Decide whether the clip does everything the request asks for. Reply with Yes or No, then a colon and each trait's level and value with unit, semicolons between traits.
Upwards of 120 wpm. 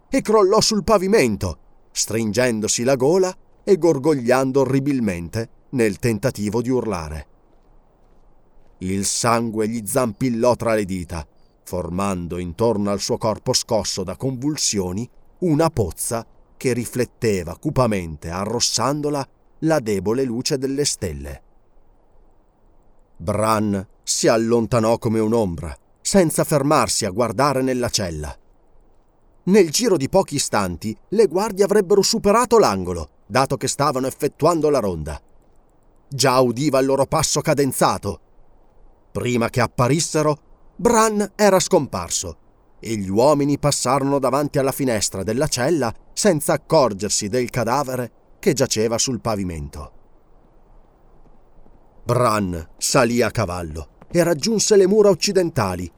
No: slow, 115 wpm